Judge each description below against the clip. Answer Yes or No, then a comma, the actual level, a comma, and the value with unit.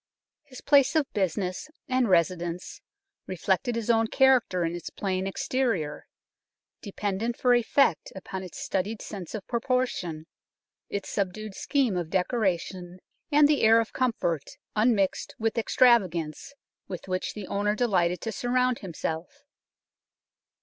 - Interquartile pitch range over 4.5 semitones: Yes, average, 5.1 semitones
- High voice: Yes, high, 205 Hz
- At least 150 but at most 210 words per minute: No, slow, 135 wpm